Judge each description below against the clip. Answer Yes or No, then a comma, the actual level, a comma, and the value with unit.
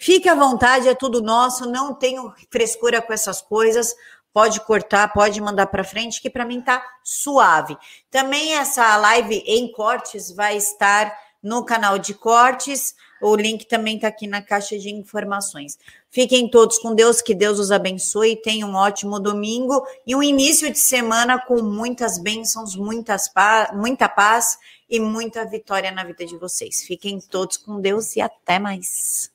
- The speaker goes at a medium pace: Yes, average, 165 wpm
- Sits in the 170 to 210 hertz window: No, high, 220 Hz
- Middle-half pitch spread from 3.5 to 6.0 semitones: No, average, 3.0 semitones